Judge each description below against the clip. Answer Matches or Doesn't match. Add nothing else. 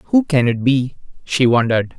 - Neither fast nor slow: Matches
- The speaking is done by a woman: Doesn't match